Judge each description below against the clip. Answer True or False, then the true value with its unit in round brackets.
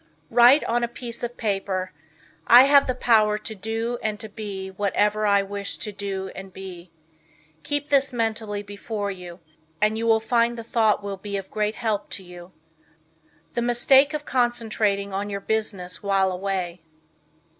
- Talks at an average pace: True (165 wpm)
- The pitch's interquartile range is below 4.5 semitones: True (3.0 semitones)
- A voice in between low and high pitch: False (210 Hz)